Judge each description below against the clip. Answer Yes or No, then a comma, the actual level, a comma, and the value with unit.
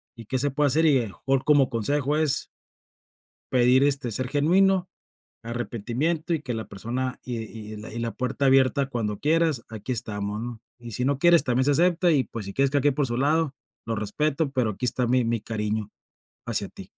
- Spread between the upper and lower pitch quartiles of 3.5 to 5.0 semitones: Yes, average, 4.0 semitones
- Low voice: Yes, low, 130 Hz